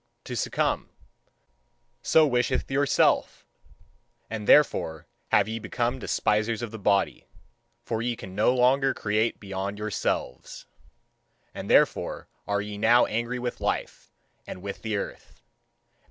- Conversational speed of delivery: No, slow, 130 wpm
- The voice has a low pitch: Yes, low, 110 Hz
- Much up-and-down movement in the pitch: No, average, 3.1 semitones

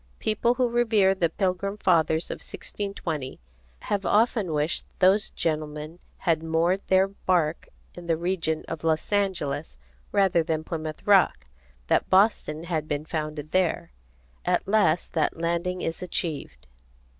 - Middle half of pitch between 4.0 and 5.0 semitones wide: No, average, 3.6 semitones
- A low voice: No, medium, 170 Hz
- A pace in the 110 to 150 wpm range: Yes, slow, 135 wpm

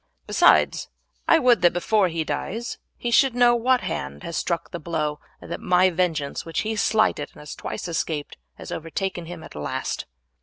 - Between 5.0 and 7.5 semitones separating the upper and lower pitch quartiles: Yes, wide, 5.5 semitones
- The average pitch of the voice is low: No, medium, 175 Hz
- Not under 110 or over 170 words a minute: No, average, 185 wpm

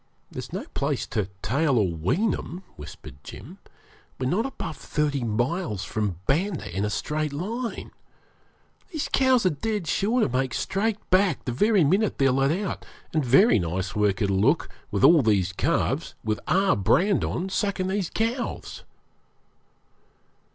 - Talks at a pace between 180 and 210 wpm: No, average, 155 wpm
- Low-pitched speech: No, medium, 150 Hz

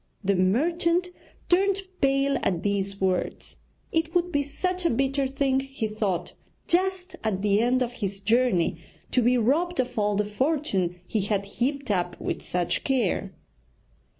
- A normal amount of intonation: No, wide, 6.8 semitones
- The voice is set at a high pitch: Yes, very high, 250 Hz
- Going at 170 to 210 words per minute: No, average, 155 wpm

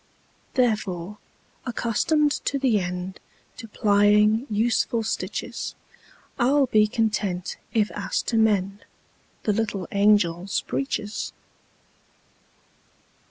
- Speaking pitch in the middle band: No, high, 210 Hz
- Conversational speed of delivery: No, slow, 80 wpm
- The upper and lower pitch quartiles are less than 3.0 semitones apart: Yes, narrow, 2.4 semitones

